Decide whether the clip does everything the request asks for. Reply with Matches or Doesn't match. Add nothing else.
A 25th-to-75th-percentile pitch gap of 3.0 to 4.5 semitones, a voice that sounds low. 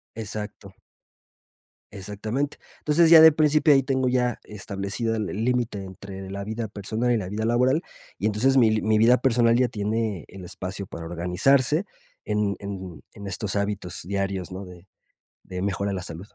Matches